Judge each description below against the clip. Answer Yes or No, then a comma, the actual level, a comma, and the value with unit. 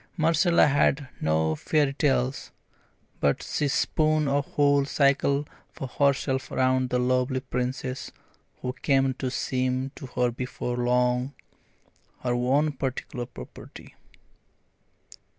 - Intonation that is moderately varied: No, narrow, 2.2 semitones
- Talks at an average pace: No, slow, 115 wpm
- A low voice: Yes, low, 130 Hz